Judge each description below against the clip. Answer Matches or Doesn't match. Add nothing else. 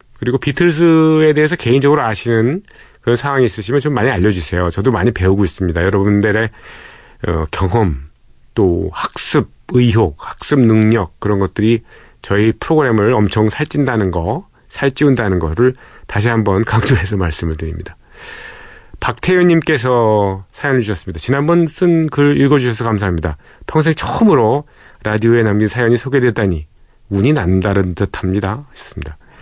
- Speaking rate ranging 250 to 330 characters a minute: Doesn't match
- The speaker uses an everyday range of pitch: Doesn't match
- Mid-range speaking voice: Doesn't match